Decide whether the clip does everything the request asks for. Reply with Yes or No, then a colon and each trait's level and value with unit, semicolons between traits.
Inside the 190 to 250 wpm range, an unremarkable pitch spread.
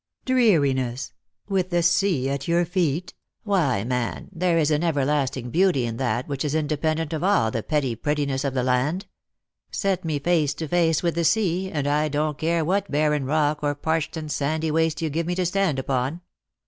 Yes: average, 195 wpm; average, 3.7 semitones